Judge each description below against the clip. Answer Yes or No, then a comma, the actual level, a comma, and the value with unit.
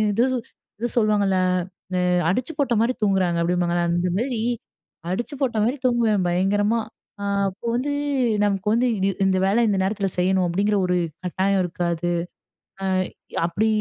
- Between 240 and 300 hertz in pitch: No, high, 195 Hz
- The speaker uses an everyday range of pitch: Yes, average, 3.9 semitones